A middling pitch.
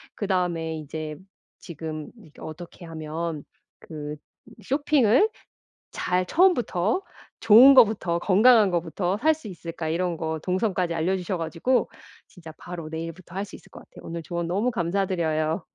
Yes: medium, 175 Hz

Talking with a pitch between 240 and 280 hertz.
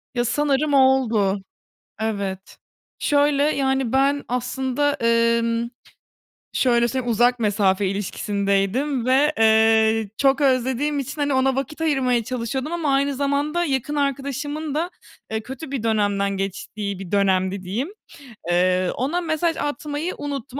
Yes: very high, 255 Hz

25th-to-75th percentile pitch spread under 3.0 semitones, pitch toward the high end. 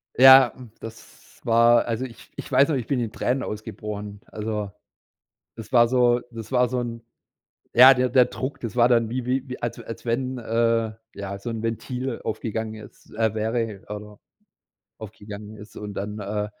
No: narrow, 2.6 semitones; low, 115 Hz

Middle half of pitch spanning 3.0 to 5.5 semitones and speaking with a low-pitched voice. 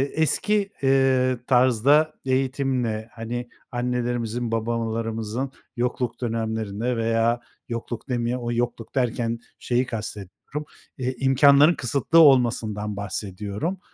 No: narrow, 2.6 semitones; low, 120 Hz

